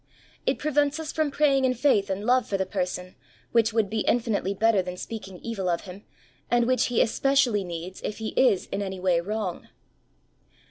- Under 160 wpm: No, average, 190 wpm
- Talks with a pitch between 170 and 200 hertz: No, high, 215 Hz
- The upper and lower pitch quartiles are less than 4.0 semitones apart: No, average, 4.9 semitones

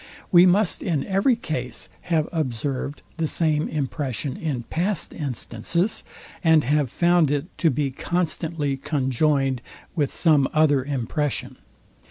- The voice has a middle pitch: Yes, medium, 150 Hz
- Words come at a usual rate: No, slow, 125 wpm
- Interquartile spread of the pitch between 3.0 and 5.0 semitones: Yes, average, 3.6 semitones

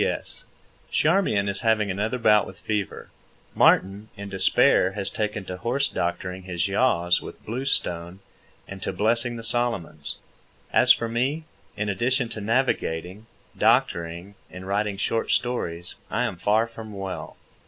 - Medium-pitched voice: No, low, 105 Hz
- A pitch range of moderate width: Yes, average, 3.7 semitones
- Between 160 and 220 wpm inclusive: No, average, 145 wpm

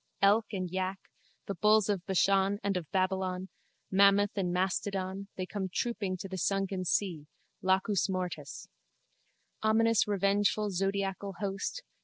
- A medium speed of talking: No, slow, 130 wpm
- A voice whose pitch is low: No, high, 195 Hz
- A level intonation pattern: Yes, narrow, 1.5 semitones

